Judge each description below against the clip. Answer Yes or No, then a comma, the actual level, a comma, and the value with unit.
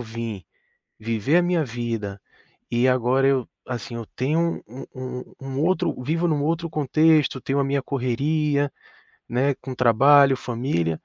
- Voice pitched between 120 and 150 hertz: Yes, low, 135 Hz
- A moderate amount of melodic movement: Yes, average, 3.8 semitones